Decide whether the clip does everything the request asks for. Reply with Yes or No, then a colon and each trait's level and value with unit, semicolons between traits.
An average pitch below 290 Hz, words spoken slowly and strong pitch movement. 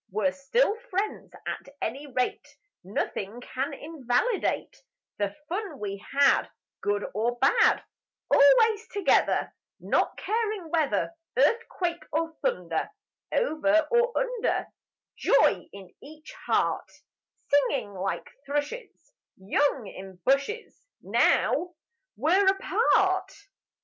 No: very high, 295 Hz; slow, 100 wpm; wide, 8.0 semitones